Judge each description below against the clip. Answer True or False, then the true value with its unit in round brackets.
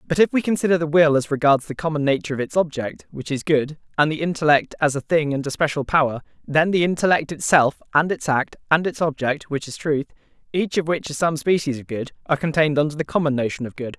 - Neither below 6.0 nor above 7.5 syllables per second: True (6.2 syllables/s)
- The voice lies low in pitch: False (150 Hz)